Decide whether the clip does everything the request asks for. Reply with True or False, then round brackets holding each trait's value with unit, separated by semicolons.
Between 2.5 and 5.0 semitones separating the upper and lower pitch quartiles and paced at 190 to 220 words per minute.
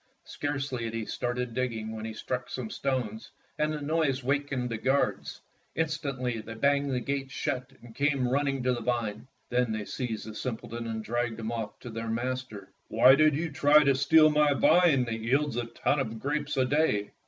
True (3.7 semitones; 195 wpm)